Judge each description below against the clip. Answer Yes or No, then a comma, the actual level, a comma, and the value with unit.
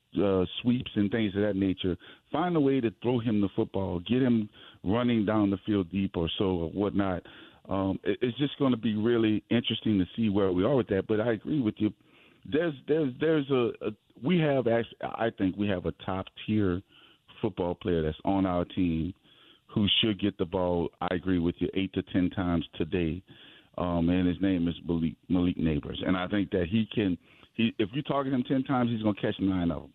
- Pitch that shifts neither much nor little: Yes, average, 4.0 semitones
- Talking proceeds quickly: Yes, fast, 220 wpm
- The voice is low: Yes, low, 100 Hz